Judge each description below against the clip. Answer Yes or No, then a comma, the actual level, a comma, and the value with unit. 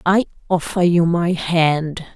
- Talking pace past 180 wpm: No, average, 140 wpm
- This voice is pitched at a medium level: Yes, medium, 170 Hz